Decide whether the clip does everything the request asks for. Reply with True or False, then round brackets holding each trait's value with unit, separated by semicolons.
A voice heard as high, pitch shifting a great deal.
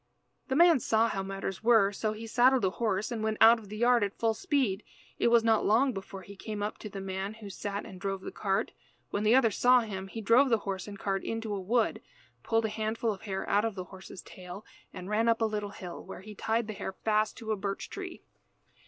False (215 Hz; 2.7 semitones)